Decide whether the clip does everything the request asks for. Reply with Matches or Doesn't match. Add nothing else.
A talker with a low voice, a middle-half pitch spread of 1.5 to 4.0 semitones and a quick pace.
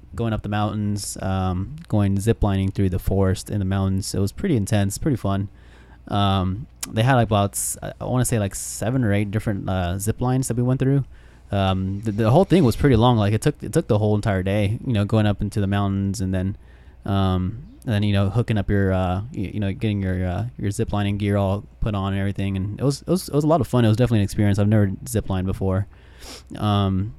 Matches